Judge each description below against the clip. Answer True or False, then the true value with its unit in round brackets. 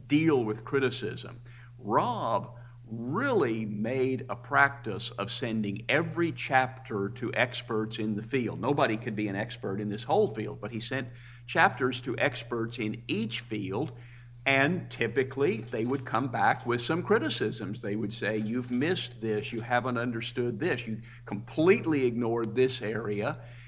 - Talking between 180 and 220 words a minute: False (150 wpm)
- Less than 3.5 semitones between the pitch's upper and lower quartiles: True (2.8 semitones)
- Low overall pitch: True (120 Hz)